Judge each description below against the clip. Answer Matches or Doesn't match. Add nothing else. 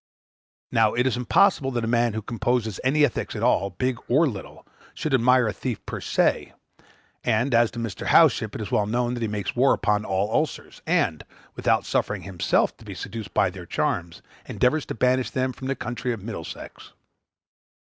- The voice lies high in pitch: Doesn't match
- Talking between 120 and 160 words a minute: Doesn't match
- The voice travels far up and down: Doesn't match